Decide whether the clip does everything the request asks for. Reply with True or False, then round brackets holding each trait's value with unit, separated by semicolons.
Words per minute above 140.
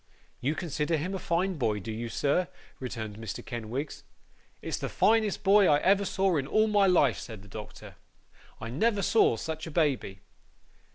True (175 wpm)